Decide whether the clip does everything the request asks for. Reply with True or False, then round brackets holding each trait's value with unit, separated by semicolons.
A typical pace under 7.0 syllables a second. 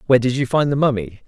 False (7.3 syllables/s)